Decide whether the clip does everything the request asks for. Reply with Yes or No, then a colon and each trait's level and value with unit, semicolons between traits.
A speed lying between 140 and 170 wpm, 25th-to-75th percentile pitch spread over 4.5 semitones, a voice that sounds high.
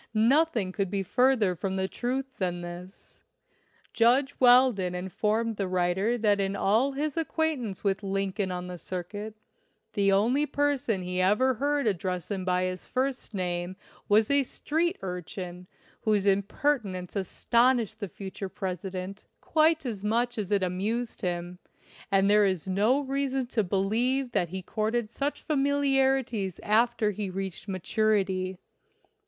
Yes: average, 145 wpm; average, 5.0 semitones; high, 205 Hz